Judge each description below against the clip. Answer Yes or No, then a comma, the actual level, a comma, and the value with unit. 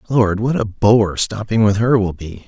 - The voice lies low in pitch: Yes, low, 105 Hz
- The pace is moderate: No, fast, 220 wpm